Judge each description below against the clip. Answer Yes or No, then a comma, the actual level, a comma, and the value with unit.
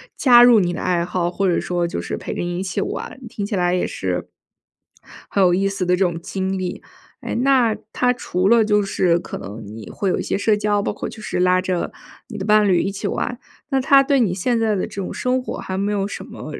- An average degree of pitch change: Yes, average, 3.6 semitones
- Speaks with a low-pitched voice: No, high, 195 Hz